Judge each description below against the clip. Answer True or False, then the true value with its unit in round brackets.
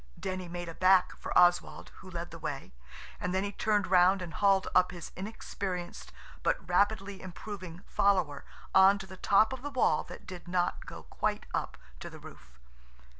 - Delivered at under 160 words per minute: False (180 wpm)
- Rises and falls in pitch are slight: True (2.1 semitones)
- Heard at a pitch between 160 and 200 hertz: True (185 Hz)